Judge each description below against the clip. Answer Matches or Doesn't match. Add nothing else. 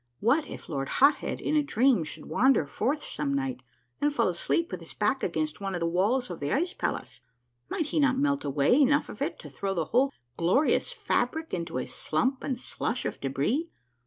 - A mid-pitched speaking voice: Doesn't match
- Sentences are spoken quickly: Matches